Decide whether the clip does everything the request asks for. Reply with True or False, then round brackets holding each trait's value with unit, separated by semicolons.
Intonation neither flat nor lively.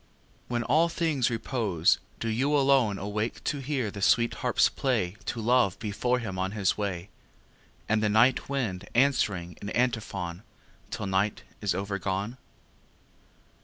True (4.2 semitones)